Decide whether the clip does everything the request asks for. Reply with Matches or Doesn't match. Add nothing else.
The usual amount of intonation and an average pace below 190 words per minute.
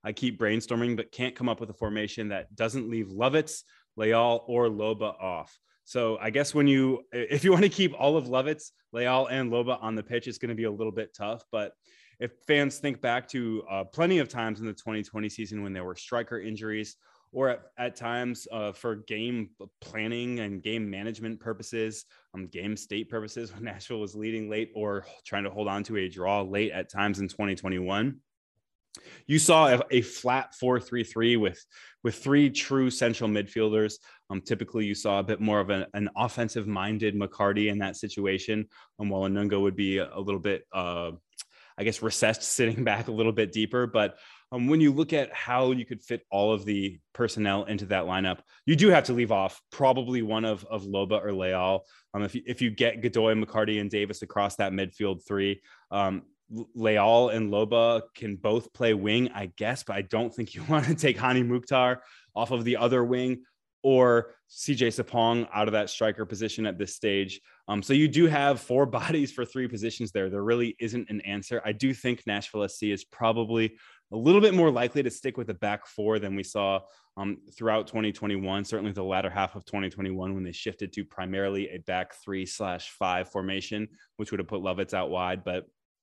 Doesn't match